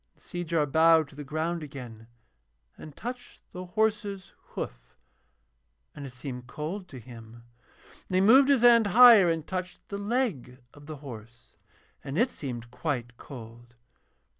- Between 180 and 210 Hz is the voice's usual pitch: No, medium, 155 Hz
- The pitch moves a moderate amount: No, wide, 8.0 semitones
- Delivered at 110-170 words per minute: Yes, average, 150 wpm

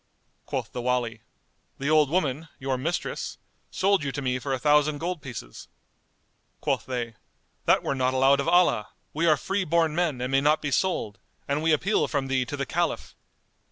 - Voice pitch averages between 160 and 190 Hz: No, medium, 140 Hz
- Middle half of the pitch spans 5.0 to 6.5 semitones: No, average, 3.9 semitones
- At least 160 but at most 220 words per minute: Yes, average, 190 wpm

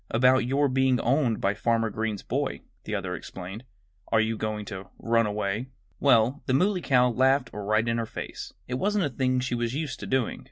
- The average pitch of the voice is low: Yes, low, 120 Hz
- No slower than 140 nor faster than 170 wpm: No, average, 200 wpm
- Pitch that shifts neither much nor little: Yes, average, 3.3 semitones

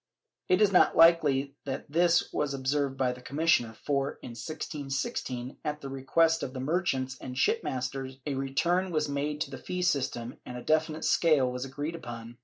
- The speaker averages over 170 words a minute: Yes, average, 180 wpm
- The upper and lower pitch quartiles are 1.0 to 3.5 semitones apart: Yes, average, 3.2 semitones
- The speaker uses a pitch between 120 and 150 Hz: Yes, medium, 140 Hz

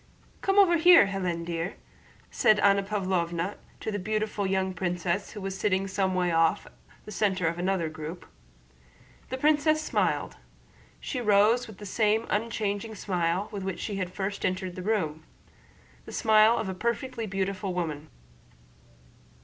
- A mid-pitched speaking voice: No, high, 195 Hz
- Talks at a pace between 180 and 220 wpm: No, average, 150 wpm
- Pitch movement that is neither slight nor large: Yes, average, 3.0 semitones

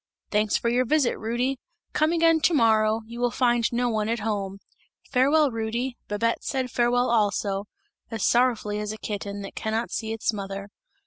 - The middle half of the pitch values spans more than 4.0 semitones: No, average, 2.8 semitones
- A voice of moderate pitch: No, high, 230 Hz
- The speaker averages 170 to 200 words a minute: Yes, average, 175 wpm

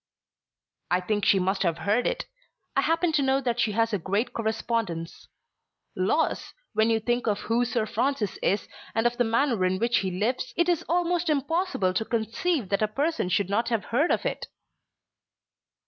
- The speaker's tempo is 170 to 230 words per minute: Yes, average, 185 wpm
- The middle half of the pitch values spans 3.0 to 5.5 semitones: Yes, average, 4.9 semitones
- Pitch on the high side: Yes, high, 230 Hz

